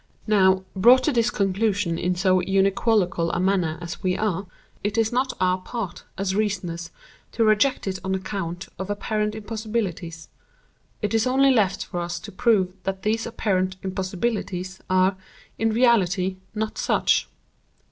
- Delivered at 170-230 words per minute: No, average, 150 wpm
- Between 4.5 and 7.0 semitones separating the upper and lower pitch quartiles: No, average, 2.9 semitones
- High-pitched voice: Yes, high, 195 Hz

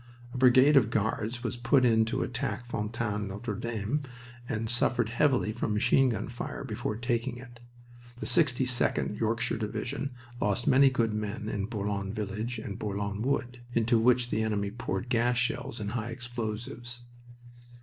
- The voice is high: No, low, 115 Hz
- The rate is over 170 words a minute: No, average, 155 wpm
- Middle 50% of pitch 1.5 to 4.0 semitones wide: Yes, narrow, 2.5 semitones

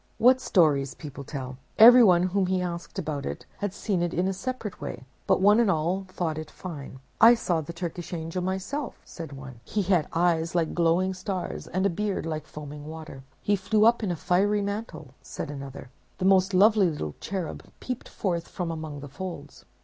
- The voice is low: No, medium, 175 Hz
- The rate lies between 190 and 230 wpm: Yes, average, 195 wpm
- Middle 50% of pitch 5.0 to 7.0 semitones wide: No, average, 4.1 semitones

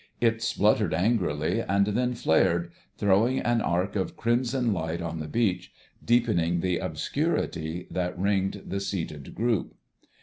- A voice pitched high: No, low, 100 Hz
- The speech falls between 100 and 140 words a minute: Yes, slow, 135 wpm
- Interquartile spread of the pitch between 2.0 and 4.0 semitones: No, average, 5.0 semitones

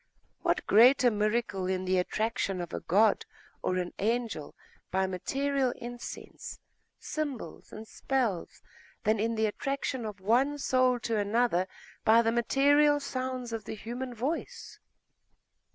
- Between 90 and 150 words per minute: Yes, slow, 135 wpm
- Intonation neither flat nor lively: Yes, average, 3.8 semitones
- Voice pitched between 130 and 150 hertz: No, high, 230 Hz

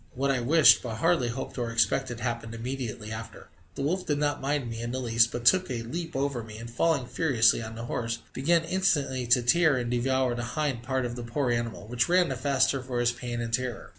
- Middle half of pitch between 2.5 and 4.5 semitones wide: Yes, average, 2.9 semitones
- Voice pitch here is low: Yes, low, 125 Hz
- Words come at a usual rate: No, fast, 230 wpm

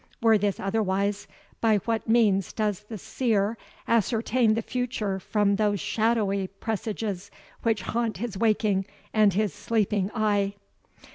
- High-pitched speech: Yes, high, 215 Hz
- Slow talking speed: Yes, slow, 130 wpm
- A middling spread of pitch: No, narrow, 2.2 semitones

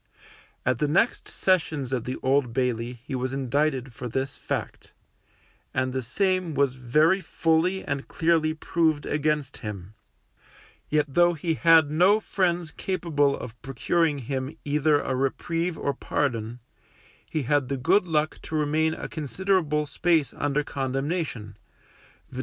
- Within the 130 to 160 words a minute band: Yes, average, 140 wpm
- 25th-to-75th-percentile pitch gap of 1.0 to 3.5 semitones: No, average, 3.9 semitones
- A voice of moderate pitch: Yes, medium, 145 Hz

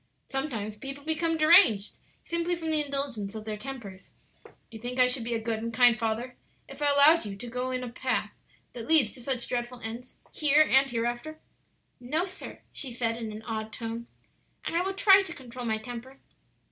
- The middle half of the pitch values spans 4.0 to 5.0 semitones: Yes, average, 4.3 semitones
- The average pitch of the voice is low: No, very high, 250 Hz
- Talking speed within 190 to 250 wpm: Yes, fast, 205 wpm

